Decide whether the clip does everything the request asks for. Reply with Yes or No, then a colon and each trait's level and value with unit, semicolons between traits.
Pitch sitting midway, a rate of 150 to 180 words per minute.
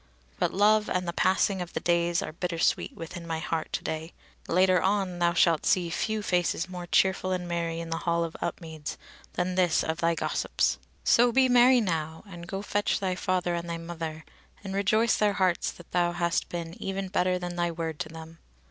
No: medium, 175 Hz; average, 200 wpm